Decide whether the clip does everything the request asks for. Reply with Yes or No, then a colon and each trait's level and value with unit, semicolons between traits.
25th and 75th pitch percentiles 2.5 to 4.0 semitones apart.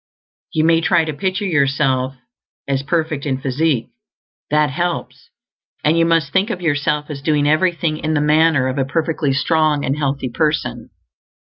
Yes: average, 2.9 semitones